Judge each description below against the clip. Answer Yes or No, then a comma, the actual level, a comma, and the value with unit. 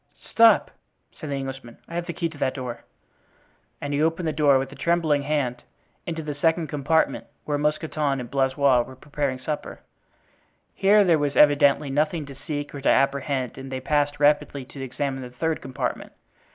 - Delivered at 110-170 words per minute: No, average, 180 wpm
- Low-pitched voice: No, medium, 145 Hz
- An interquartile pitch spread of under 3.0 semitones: Yes, narrow, 2.4 semitones